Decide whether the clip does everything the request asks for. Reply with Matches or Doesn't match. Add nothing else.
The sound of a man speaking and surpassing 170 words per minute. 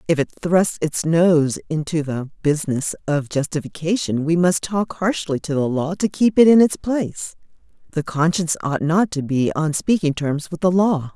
Doesn't match